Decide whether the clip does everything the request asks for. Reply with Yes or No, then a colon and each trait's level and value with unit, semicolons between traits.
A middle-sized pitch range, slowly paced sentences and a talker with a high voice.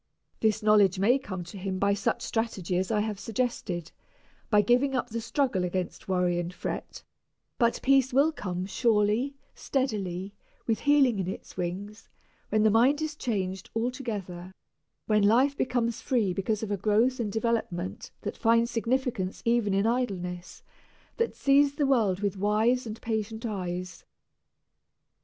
No: average, 4.2 semitones; average, 150 wpm; high, 215 Hz